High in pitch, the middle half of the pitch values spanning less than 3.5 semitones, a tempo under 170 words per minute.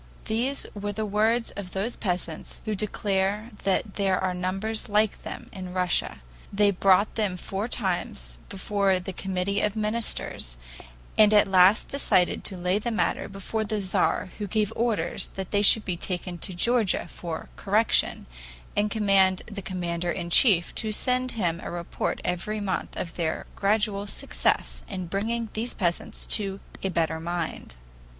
Yes: high, 195 Hz; average, 2.8 semitones; average, 155 wpm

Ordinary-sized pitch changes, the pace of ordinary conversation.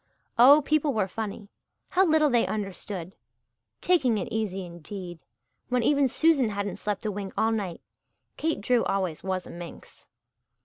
No: wide, 5.8 semitones; average, 150 wpm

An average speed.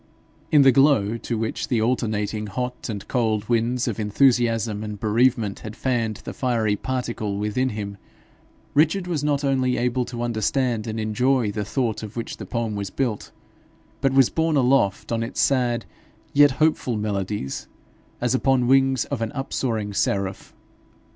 Yes: average, 160 wpm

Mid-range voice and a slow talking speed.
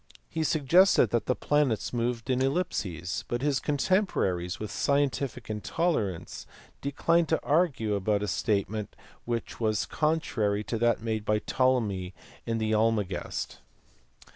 No: low, 115 Hz; slow, 130 wpm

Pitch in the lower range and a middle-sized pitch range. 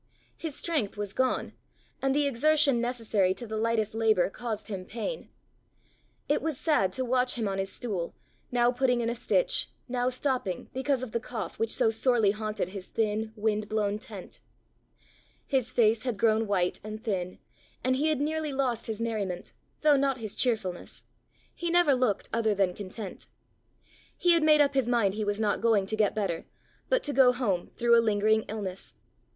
No: high, 230 Hz; average, 3.8 semitones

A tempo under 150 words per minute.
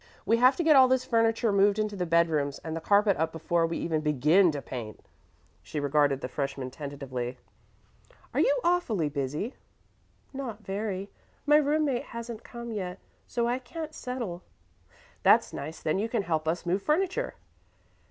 No: average, 170 wpm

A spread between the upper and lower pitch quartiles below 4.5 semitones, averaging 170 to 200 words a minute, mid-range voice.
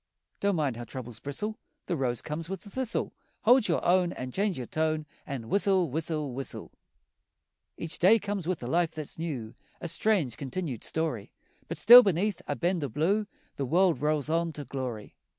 No: wide, 5.6 semitones; average, 185 wpm; medium, 160 Hz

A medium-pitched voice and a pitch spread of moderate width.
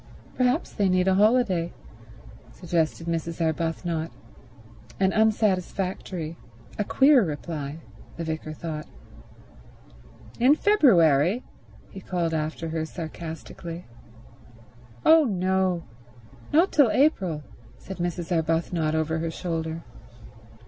Yes: medium, 170 Hz; average, 3.3 semitones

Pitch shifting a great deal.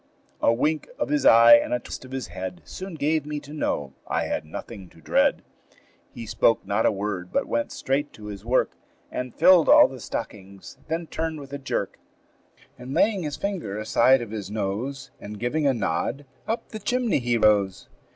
Yes: wide, 6.2 semitones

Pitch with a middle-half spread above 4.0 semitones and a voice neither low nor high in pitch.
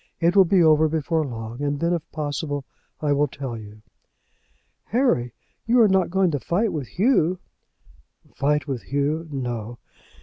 Yes: average, 4.4 semitones; medium, 150 Hz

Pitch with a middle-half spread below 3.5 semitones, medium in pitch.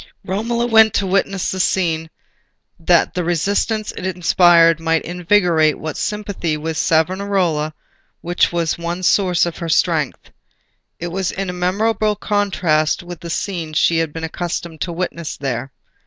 Yes: average, 2.9 semitones; medium, 175 Hz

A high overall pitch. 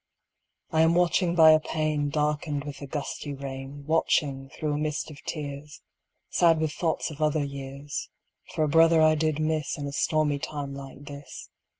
No: medium, 150 Hz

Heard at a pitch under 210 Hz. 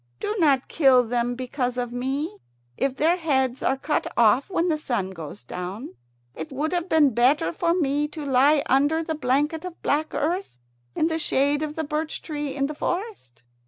No: very high, 285 Hz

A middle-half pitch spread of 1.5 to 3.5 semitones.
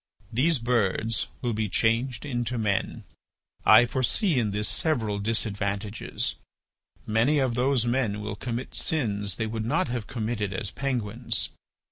Yes: average, 3.0 semitones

